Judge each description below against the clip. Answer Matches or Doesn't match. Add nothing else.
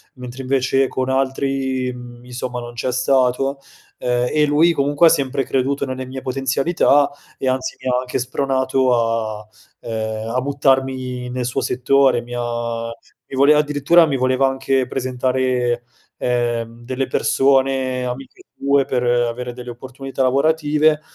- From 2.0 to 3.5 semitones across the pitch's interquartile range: Doesn't match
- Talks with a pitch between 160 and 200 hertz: Doesn't match